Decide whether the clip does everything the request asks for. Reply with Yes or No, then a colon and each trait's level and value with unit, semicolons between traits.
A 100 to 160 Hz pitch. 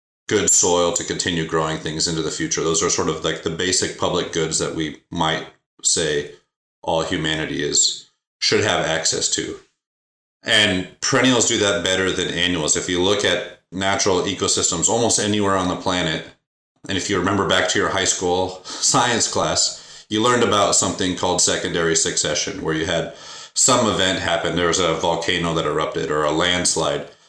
No: very low, 90 Hz